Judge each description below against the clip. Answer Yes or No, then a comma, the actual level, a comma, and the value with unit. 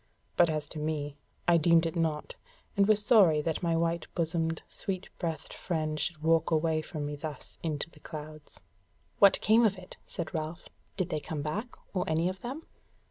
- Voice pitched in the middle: Yes, medium, 165 Hz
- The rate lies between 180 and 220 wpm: Yes, average, 190 wpm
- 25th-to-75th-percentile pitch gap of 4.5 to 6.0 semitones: No, narrow, 2.6 semitones